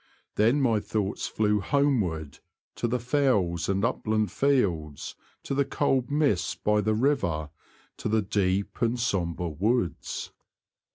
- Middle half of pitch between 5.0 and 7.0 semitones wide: Yes, wide, 5.4 semitones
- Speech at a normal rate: No, slow, 130 wpm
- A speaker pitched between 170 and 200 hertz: No, low, 110 Hz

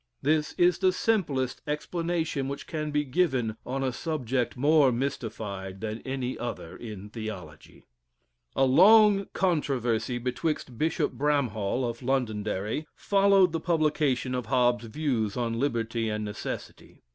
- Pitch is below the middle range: Yes, low, 130 Hz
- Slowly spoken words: Yes, slow, 130 wpm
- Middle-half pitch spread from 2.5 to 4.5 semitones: No, average, 5.1 semitones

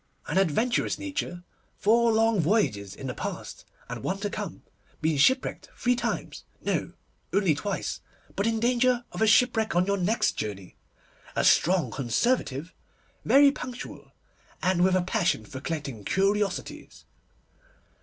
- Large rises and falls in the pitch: Yes, wide, 6.3 semitones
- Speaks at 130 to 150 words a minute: Yes, average, 140 wpm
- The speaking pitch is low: No, high, 195 Hz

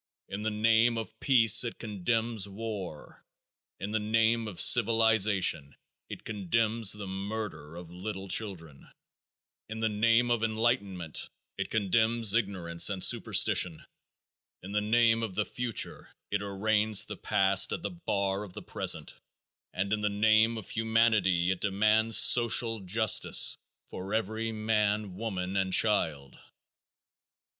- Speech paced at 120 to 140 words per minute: Yes, slow, 135 wpm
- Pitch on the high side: No, low, 105 Hz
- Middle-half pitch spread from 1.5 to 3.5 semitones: Yes, narrow, 2.6 semitones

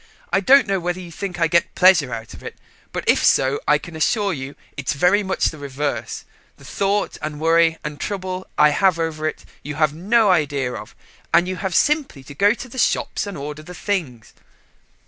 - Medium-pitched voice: Yes, medium, 165 Hz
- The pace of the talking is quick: Yes, fast, 210 wpm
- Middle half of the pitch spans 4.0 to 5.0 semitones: Yes, average, 4.7 semitones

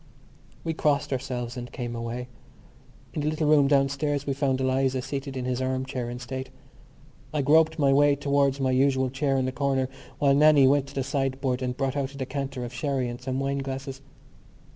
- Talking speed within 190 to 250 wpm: Yes, average, 200 wpm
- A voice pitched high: No, low, 135 Hz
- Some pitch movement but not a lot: No, narrow, 1.5 semitones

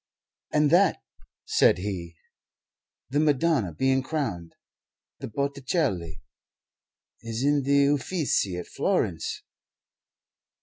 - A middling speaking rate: No, slow, 90 wpm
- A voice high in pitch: No, low, 135 Hz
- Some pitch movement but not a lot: No, wide, 7.7 semitones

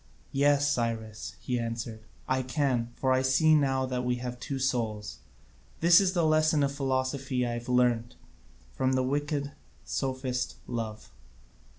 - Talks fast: No, average, 155 wpm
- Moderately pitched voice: No, low, 130 Hz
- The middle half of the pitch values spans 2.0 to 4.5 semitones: Yes, average, 2.7 semitones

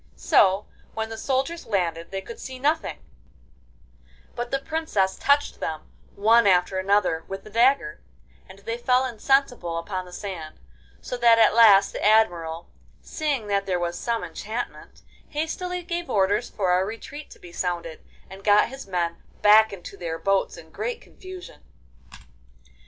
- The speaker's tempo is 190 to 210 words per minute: No, average, 155 wpm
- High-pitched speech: Yes, high, 210 Hz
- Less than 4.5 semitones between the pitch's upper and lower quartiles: No, wide, 5.6 semitones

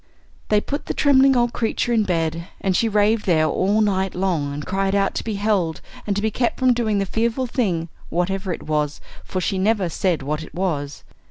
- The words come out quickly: Yes, fast, 220 wpm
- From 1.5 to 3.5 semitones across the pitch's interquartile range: No, average, 4.6 semitones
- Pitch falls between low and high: No, high, 195 Hz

